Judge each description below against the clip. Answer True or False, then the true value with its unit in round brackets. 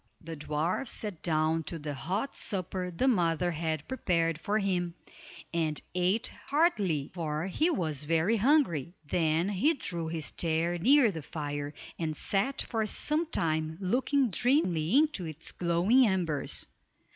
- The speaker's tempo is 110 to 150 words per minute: True (140 wpm)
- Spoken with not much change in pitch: False (5.4 semitones)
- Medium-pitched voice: True (175 Hz)